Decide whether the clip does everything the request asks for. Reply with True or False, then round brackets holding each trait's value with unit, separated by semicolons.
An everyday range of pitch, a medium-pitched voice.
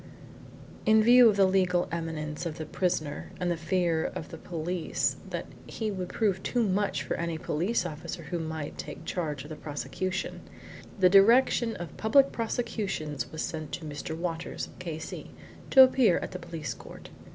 True (4.0 semitones; 175 Hz)